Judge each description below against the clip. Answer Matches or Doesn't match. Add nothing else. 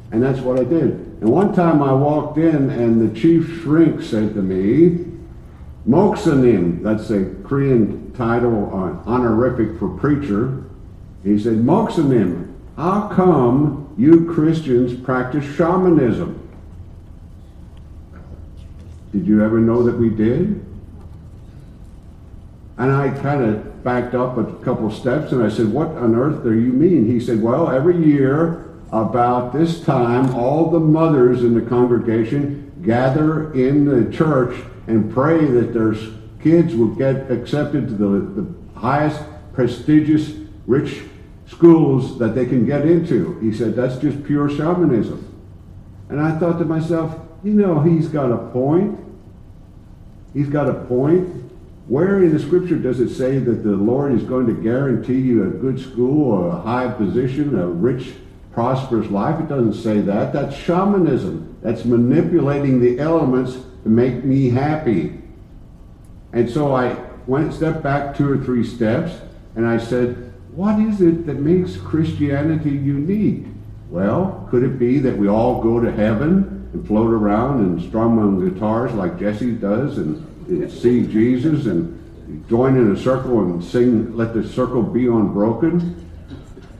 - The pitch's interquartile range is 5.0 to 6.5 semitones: Matches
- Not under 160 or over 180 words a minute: Doesn't match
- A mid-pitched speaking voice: Doesn't match